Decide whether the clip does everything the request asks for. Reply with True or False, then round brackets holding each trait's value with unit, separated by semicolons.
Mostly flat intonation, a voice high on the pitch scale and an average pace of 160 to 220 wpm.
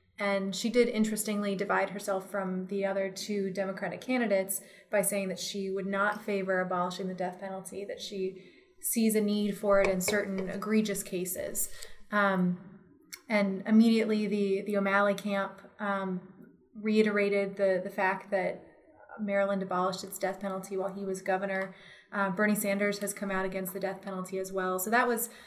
True (1.3 semitones; 195 Hz; 165 wpm)